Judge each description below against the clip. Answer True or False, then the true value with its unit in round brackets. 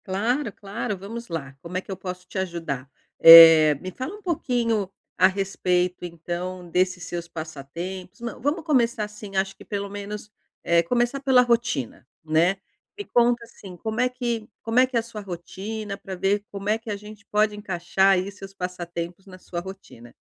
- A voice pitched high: True (195 Hz)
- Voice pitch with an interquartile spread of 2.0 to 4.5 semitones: True (4.1 semitones)